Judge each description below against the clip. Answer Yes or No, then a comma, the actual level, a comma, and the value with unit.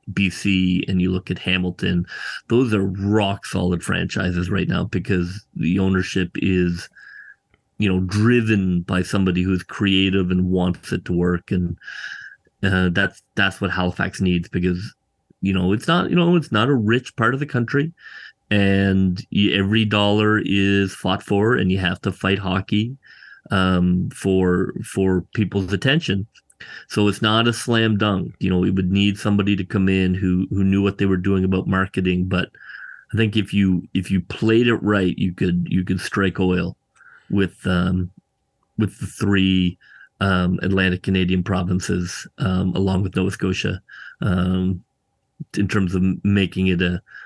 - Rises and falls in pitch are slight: Yes, narrow, 1.8 semitones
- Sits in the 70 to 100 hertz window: Yes, very low, 95 Hz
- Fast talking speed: No, average, 165 wpm